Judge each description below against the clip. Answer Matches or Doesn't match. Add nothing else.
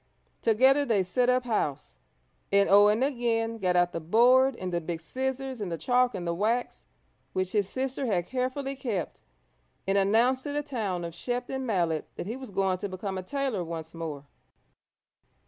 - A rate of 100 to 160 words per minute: Doesn't match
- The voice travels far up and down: Matches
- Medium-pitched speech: Doesn't match